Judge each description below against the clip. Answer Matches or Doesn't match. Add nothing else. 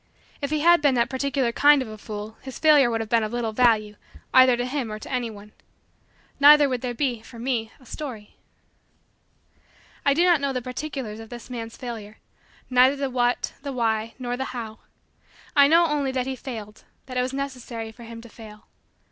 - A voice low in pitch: Doesn't match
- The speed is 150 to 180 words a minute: Doesn't match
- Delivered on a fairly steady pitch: Doesn't match